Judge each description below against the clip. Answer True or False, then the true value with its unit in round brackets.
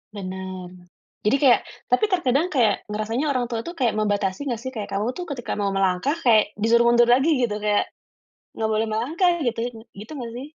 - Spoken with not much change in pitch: False (3.4 semitones)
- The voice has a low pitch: False (230 Hz)